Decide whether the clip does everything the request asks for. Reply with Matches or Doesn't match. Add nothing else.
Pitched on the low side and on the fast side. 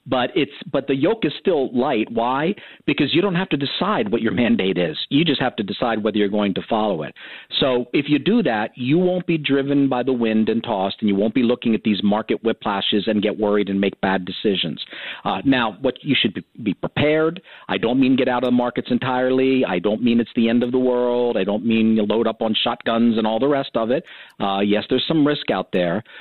Matches